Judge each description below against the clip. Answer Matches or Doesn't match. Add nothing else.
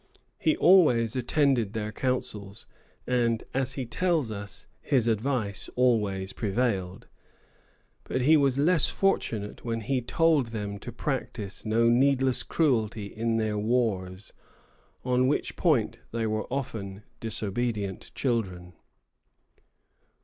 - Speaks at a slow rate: Matches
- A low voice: Matches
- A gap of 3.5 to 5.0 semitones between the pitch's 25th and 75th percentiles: Matches